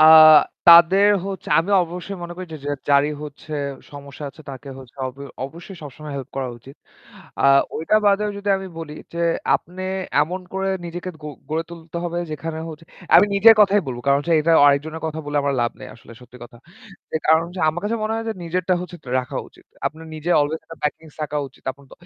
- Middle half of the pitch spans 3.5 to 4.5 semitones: Yes, average, 4.0 semitones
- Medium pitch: Yes, medium, 160 Hz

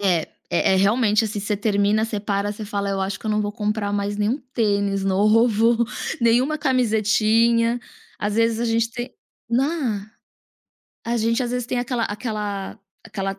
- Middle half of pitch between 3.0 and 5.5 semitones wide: No, narrow, 2.4 semitones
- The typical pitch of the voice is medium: No, high, 215 Hz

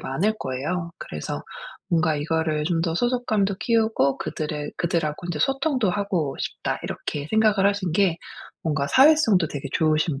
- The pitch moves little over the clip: No, average, 5.3 semitones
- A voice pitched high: No, medium, 170 Hz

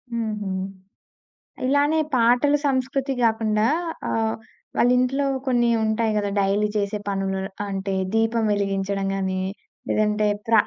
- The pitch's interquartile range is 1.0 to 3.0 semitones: No, average, 3.5 semitones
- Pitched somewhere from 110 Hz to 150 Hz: No, high, 220 Hz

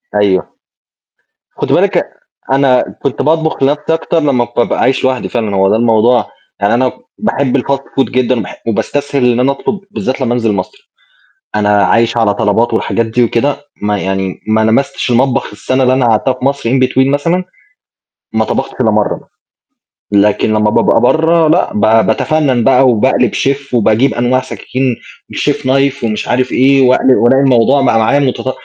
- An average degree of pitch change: Yes, average, 3.5 semitones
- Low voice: Yes, low, 125 Hz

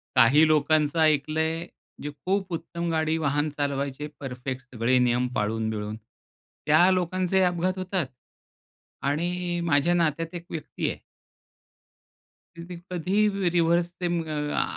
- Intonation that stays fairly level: No, average, 3.6 semitones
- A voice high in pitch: No, medium, 160 Hz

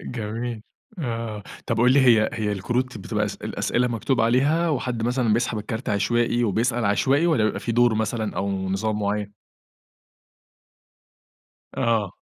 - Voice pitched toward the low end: Yes, low, 115 Hz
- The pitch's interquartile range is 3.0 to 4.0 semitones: No, narrow, 2.6 semitones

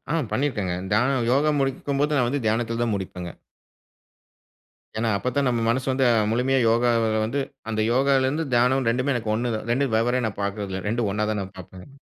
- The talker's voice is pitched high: No, low, 120 Hz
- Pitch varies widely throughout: No, average, 3.5 semitones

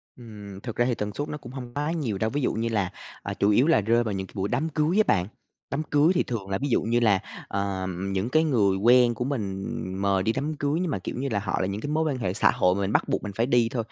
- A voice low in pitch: Yes, low, 115 Hz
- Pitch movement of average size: No, wide, 5.9 semitones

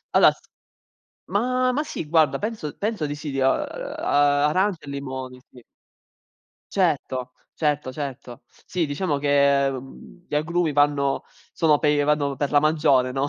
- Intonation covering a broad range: No, narrow, 2.6 semitones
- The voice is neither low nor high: Yes, medium, 145 Hz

